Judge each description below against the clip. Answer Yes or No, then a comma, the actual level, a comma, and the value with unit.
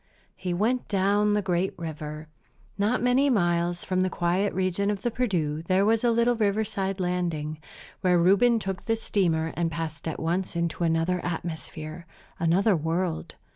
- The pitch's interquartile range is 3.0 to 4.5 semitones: Yes, average, 3.6 semitones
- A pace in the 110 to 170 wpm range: Yes, average, 160 wpm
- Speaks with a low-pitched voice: No, medium, 180 Hz